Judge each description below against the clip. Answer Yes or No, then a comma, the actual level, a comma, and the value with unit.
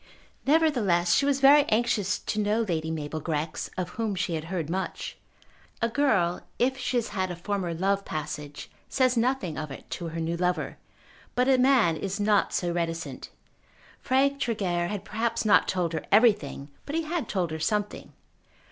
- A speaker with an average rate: Yes, average, 175 wpm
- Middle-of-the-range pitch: No, high, 195 Hz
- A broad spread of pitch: Yes, wide, 5.9 semitones